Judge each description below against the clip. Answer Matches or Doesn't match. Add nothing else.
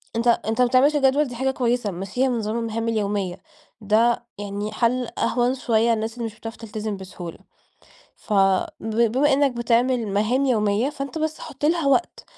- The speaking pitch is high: Matches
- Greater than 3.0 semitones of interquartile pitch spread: Matches